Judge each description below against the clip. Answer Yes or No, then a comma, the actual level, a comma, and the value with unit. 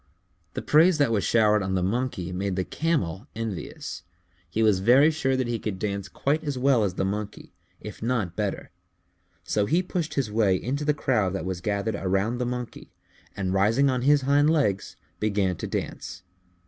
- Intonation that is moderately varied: No, wide, 5.7 semitones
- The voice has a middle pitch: No, low, 110 Hz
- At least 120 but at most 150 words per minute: No, average, 185 wpm